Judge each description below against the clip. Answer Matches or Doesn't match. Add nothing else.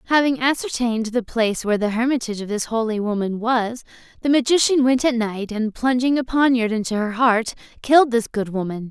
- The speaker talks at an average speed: Matches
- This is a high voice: Matches